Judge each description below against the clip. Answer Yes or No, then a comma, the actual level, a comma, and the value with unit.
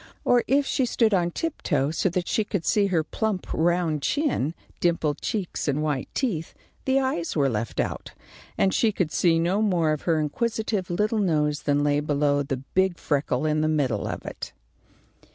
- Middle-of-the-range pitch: Yes, medium, 170 Hz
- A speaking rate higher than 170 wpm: Yes, average, 185 wpm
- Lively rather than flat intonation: Yes, wide, 5.7 semitones